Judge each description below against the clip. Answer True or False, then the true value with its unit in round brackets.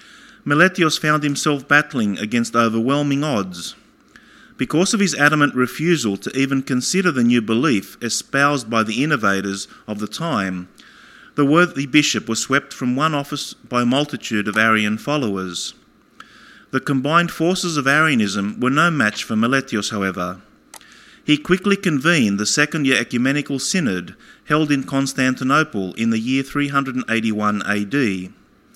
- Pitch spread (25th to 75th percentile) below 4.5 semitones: False (5.1 semitones)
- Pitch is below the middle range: True (130 Hz)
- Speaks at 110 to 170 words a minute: True (140 wpm)